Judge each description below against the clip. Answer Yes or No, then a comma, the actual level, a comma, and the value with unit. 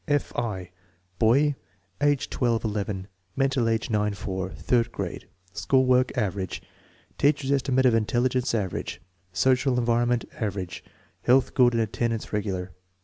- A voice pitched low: Yes, low, 115 Hz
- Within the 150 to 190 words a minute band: No, slow, 135 wpm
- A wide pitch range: No, average, 3.9 semitones